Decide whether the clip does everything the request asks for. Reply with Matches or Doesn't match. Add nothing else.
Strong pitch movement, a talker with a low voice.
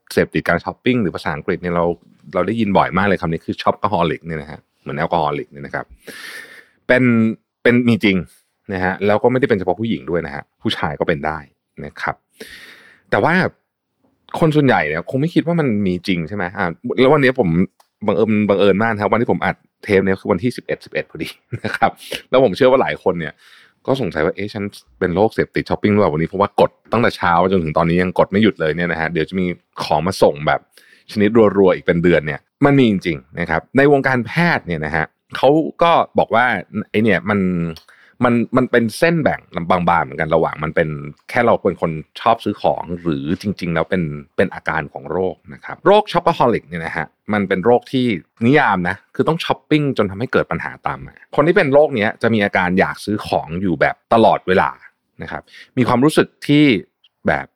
Matches